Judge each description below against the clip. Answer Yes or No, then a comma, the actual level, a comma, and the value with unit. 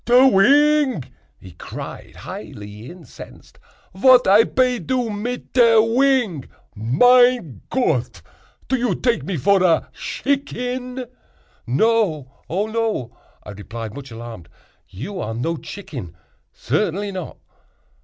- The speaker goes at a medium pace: No, slow, 110 wpm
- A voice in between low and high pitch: No, high, 200 Hz